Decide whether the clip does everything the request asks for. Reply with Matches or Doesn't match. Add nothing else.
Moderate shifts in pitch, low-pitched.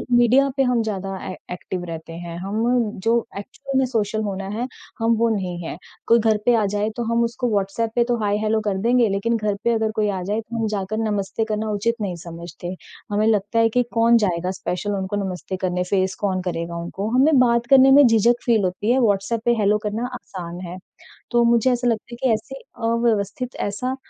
Doesn't match